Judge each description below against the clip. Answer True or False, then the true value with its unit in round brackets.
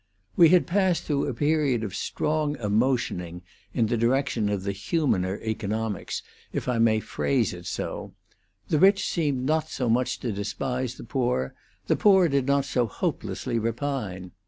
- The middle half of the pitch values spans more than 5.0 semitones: True (5.4 semitones)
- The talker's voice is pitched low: True (125 Hz)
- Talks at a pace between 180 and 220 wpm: False (160 wpm)